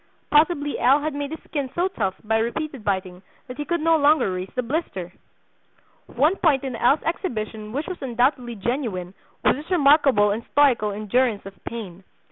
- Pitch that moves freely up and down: Yes, wide, 5.8 semitones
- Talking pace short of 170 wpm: No, average, 175 wpm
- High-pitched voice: Yes, very high, 255 Hz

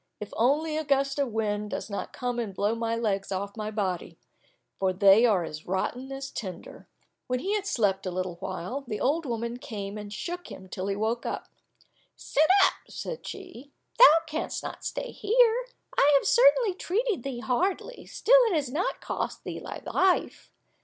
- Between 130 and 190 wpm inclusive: Yes, average, 180 wpm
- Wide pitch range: Yes, wide, 7.9 semitones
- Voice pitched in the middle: No, high, 245 Hz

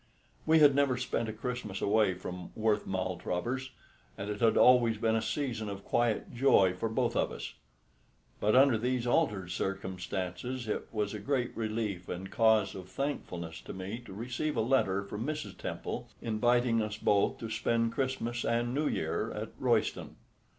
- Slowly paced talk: No, average, 170 wpm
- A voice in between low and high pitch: No, low, 110 Hz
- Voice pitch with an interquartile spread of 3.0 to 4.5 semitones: Yes, average, 3.7 semitones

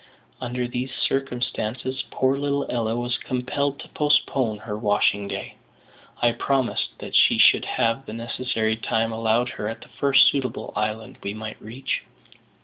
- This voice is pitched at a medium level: No, low, 120 Hz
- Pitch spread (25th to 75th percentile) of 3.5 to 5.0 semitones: No, average, 3.0 semitones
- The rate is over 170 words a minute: No, average, 150 wpm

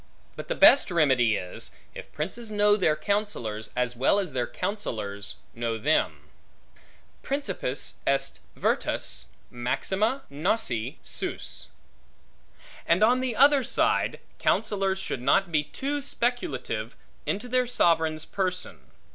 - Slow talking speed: Yes, slow, 120 wpm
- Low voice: No, medium, 185 Hz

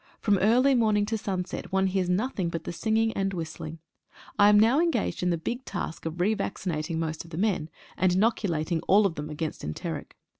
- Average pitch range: Yes, average, 4.6 semitones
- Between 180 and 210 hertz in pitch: Yes, high, 190 Hz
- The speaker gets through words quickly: Yes, fast, 210 wpm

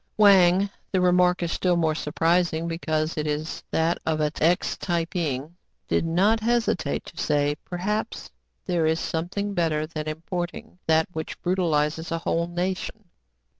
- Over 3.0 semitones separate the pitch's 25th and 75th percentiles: No, narrow, 2.4 semitones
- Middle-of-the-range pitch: Yes, medium, 170 Hz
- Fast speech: No, average, 155 wpm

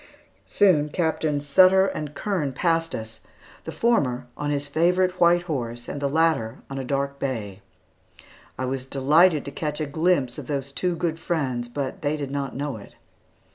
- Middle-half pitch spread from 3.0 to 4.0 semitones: Yes, average, 3.7 semitones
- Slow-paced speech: No, average, 175 wpm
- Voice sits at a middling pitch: Yes, medium, 145 Hz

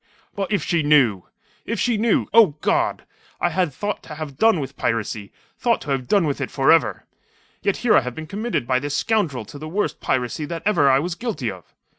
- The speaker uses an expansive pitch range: Yes, wide, 7.3 semitones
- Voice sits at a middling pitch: Yes, medium, 155 Hz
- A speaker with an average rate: No, fast, 220 wpm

